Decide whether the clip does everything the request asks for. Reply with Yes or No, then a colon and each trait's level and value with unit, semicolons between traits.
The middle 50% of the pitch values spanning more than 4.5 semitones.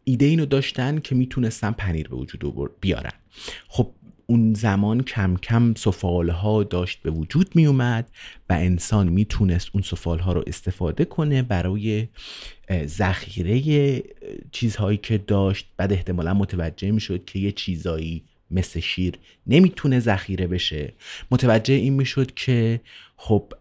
Yes: wide, 5.6 semitones